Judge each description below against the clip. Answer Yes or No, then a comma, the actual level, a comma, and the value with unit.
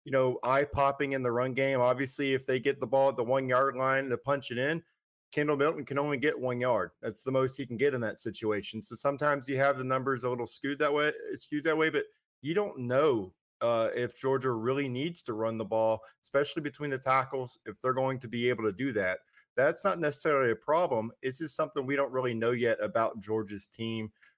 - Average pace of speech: No, fast, 235 wpm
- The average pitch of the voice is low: Yes, low, 130 Hz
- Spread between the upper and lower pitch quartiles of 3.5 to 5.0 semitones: No, average, 2.7 semitones